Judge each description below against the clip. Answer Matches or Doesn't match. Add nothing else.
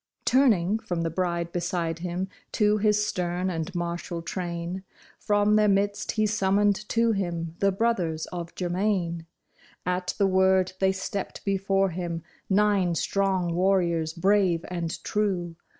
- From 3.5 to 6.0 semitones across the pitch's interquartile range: Doesn't match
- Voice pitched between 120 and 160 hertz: Doesn't match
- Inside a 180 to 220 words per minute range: Doesn't match